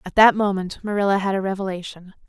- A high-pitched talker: Yes, high, 195 Hz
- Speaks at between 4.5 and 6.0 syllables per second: No, 6.4 syllables/s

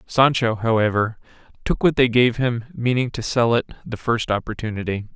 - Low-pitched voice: Yes, low, 115 Hz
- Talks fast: No, average, 165 wpm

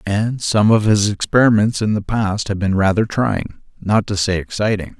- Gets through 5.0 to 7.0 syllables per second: No, 4.7 syllables/s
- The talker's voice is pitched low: Yes, low, 105 Hz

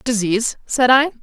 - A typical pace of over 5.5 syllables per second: No, 4.9 syllables/s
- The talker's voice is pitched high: Yes, high, 240 Hz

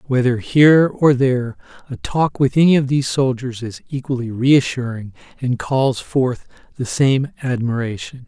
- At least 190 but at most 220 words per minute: No, average, 145 wpm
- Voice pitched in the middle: No, low, 130 Hz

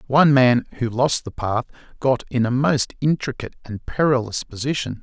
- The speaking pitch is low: Yes, low, 125 Hz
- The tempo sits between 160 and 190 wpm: Yes, average, 165 wpm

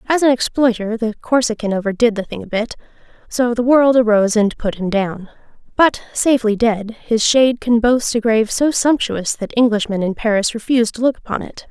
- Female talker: Yes, female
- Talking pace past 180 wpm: Yes, average, 190 wpm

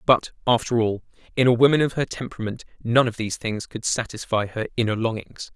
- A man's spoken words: Yes, male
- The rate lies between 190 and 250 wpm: Yes, average, 195 wpm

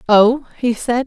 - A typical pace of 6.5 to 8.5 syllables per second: No, 3.5 syllables/s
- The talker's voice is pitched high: Yes, high, 240 Hz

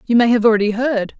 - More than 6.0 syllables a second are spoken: Yes, 6.4 syllables/s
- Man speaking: No, female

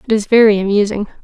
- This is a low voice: No, high, 210 Hz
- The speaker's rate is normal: Yes, average, 195 wpm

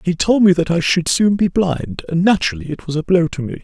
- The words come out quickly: Yes, fast, 280 wpm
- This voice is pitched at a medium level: Yes, medium, 170 Hz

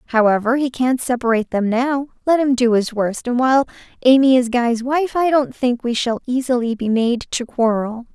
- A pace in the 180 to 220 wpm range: Yes, average, 200 wpm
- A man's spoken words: No, female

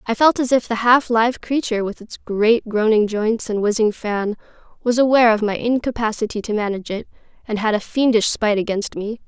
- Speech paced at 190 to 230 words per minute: Yes, average, 200 wpm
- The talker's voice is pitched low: No, high, 225 Hz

